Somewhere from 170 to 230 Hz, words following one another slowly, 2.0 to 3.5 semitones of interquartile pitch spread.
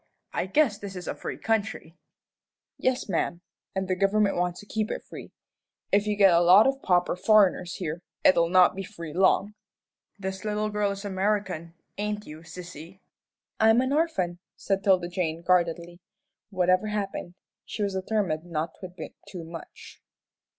No: high, 190 Hz; average, 165 wpm; average, 3.0 semitones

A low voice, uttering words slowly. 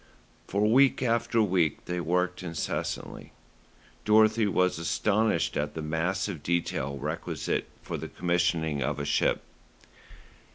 Yes: very low, 90 Hz; slow, 125 wpm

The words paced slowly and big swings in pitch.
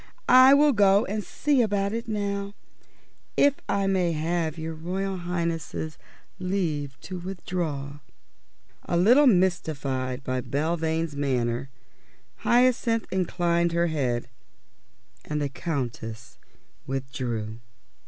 Yes: slow, 105 wpm; wide, 5.7 semitones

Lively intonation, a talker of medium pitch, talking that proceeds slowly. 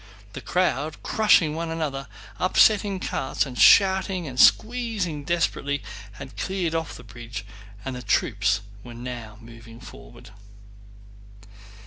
Yes: wide, 7.2 semitones; medium, 145 Hz; slow, 120 wpm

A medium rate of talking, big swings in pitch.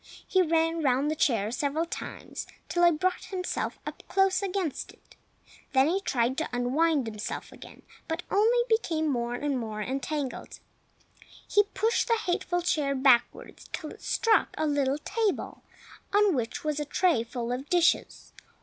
Yes: average, 160 wpm; wide, 5.7 semitones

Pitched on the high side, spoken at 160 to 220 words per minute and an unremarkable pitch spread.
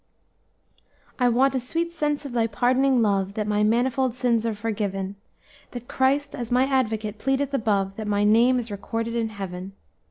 Yes: high, 230 Hz; average, 170 wpm; average, 3.8 semitones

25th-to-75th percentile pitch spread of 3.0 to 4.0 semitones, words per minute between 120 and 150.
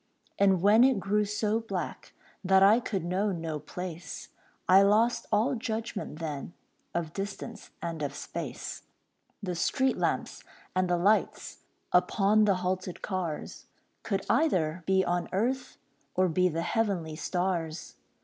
Yes: average, 3.4 semitones; average, 140 wpm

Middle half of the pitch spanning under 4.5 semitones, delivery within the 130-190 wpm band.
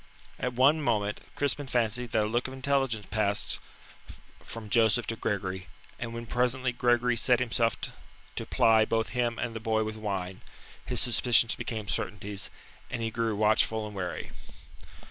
Yes: narrow, 2.4 semitones; average, 160 wpm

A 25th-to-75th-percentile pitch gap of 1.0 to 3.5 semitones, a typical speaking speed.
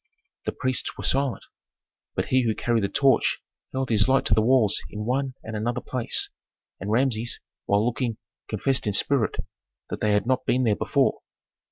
Yes: average, 3.2 semitones; average, 180 wpm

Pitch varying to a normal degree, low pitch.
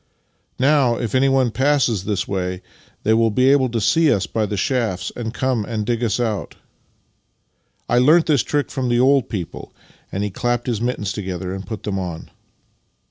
Yes: average, 4.1 semitones; low, 115 Hz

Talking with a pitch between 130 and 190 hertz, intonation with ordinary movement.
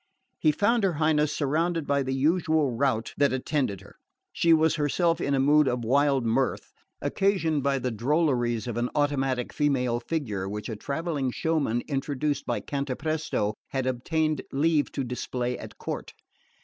Yes: medium, 140 Hz; average, 3.8 semitones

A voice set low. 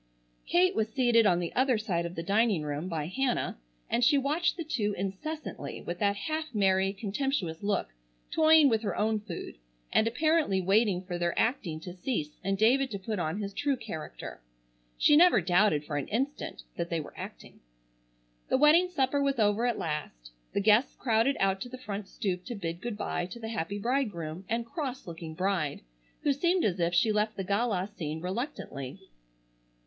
No: high, 205 Hz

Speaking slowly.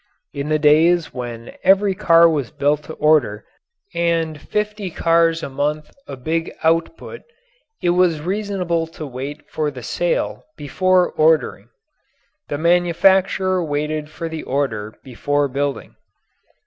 Yes: slow, 130 wpm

